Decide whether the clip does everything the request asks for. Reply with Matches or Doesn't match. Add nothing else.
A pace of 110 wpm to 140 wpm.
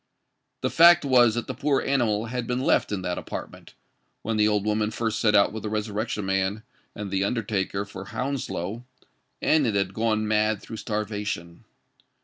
Doesn't match